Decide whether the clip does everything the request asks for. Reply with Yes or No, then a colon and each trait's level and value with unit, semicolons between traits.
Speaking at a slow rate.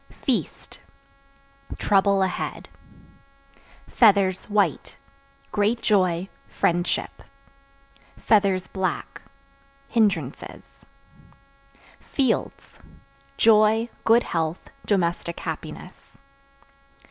Yes: slow, 55 wpm